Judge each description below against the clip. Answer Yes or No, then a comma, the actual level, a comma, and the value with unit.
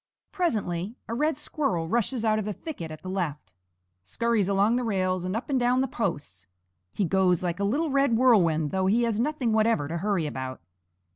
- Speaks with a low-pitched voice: No, high, 205 Hz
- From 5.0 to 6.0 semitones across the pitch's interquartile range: Yes, wide, 5.6 semitones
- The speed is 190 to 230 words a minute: Yes, average, 200 wpm